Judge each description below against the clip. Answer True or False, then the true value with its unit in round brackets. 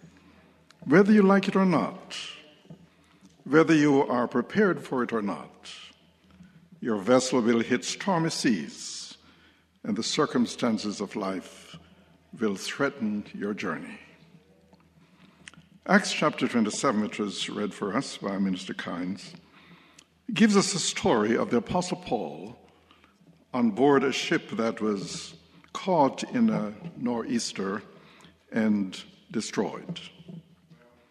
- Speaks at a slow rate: True (115 wpm)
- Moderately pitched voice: True (150 Hz)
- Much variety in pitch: True (8.2 semitones)